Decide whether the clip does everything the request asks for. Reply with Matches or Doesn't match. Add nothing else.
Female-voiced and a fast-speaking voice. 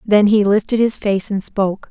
Matches